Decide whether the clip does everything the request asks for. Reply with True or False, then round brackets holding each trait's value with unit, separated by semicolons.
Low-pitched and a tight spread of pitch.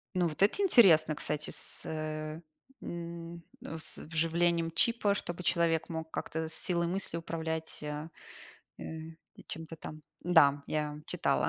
False (165 Hz; 1.7 semitones)